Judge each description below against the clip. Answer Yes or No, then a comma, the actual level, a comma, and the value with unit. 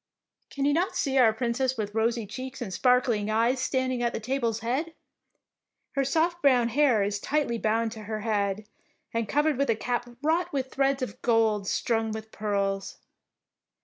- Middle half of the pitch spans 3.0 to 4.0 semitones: Yes, average, 3.6 semitones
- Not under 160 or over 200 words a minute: Yes, average, 180 wpm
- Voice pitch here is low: No, high, 240 Hz